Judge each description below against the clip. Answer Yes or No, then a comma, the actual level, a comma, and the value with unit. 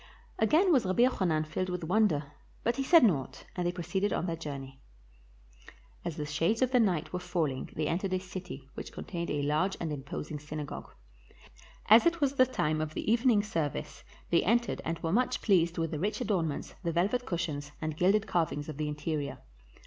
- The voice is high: No, medium, 170 Hz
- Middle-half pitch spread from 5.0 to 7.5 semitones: Yes, wide, 5.6 semitones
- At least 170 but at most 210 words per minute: Yes, average, 190 wpm